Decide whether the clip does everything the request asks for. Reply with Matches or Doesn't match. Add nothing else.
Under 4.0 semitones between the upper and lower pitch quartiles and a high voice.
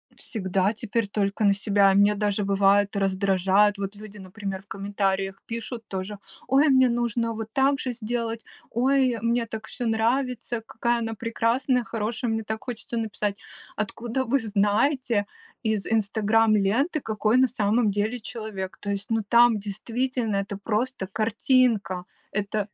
Matches